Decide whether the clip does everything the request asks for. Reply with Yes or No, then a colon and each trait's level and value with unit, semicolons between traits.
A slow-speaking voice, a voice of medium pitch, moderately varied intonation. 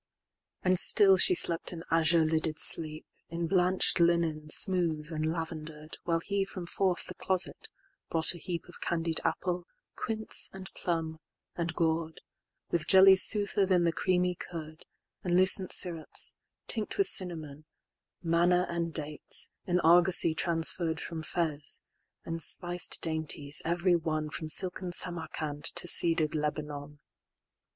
No: slow, 120 wpm; medium, 170 Hz; narrow, 2.1 semitones